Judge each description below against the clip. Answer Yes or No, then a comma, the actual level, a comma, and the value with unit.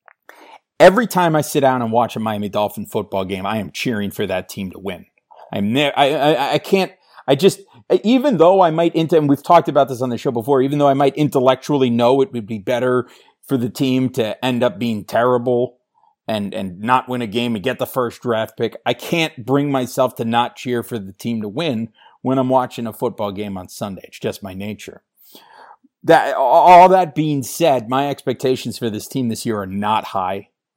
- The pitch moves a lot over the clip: No, average, 4.7 semitones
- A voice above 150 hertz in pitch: No, low, 130 Hz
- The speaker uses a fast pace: Yes, fast, 215 wpm